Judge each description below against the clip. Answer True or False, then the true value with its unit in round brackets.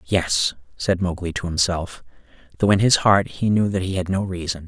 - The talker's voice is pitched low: True (90 Hz)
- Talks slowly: False (205 wpm)